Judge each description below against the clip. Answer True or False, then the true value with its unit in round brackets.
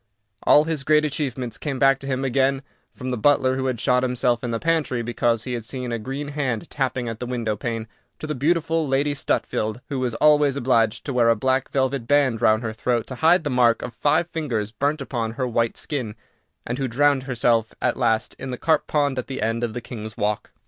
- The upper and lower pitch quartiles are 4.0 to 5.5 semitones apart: False (3.3 semitones)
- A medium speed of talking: False (225 wpm)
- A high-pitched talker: False (130 Hz)